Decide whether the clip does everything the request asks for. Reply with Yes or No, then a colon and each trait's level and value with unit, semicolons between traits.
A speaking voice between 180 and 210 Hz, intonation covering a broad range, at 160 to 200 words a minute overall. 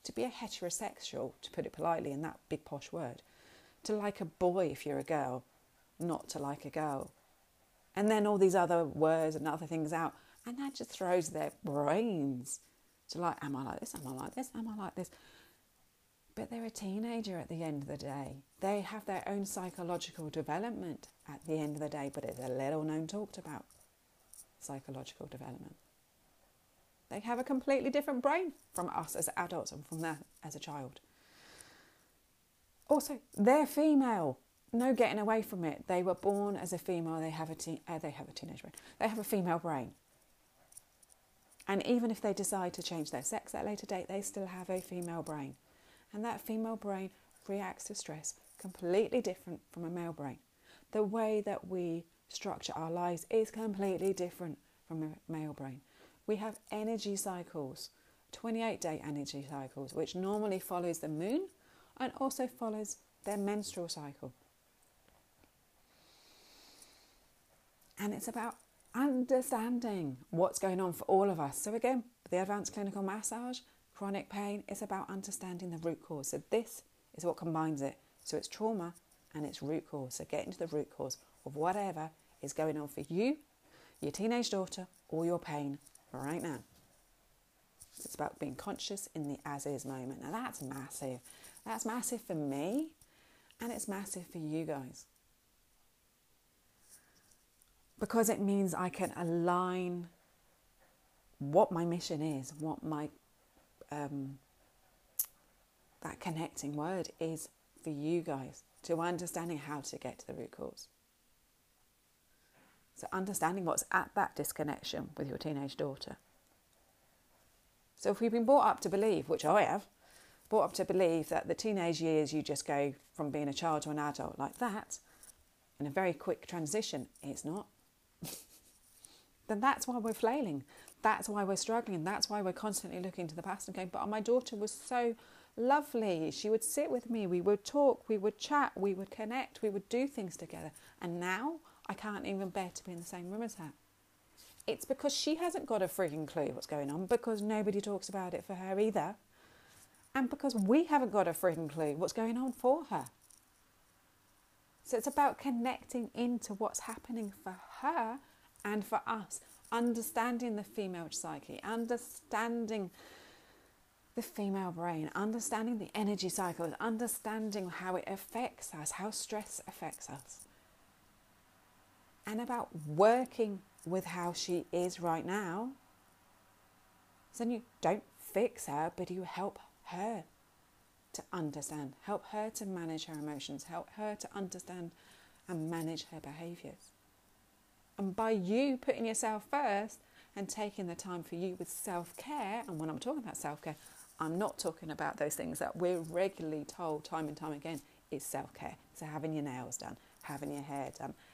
Yes: medium, 185 Hz; wide, 5.7 semitones; average, 165 wpm